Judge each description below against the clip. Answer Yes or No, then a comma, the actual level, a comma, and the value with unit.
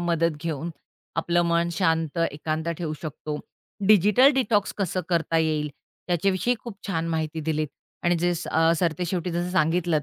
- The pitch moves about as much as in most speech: No, narrow, 2.1 semitones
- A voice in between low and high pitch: Yes, medium, 170 Hz